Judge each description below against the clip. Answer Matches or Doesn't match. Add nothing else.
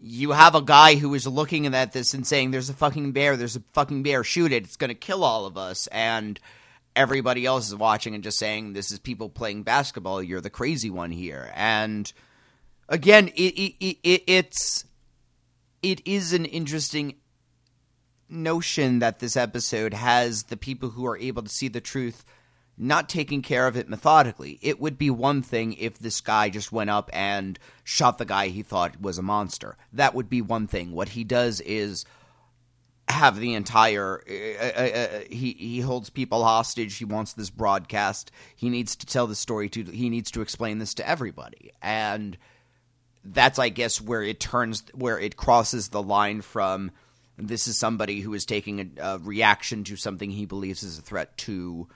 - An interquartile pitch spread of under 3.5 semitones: Doesn't match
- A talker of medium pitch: Doesn't match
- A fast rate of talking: Doesn't match